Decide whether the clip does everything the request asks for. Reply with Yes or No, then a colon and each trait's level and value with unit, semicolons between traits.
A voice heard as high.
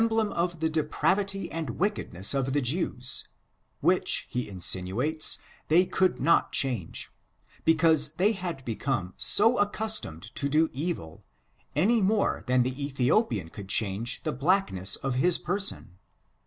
No: medium, 150 Hz